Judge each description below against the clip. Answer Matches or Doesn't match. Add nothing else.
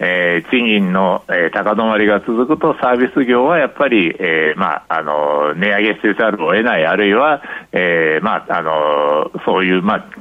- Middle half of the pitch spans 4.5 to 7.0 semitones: Matches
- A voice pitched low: Matches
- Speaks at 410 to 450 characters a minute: Doesn't match